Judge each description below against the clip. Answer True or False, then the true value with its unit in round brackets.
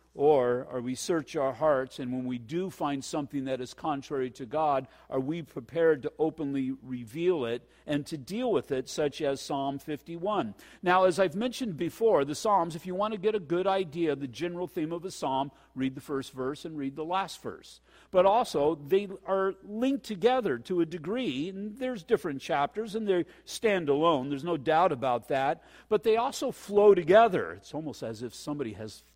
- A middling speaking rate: False (210 wpm)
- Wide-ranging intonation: True (6.0 semitones)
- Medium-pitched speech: True (165 Hz)